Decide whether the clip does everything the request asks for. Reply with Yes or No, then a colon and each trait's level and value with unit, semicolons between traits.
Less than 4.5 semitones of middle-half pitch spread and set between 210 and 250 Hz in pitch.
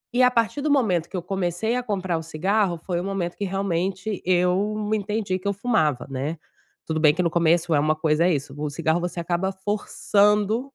No: average, 3.7 semitones; medium, 185 Hz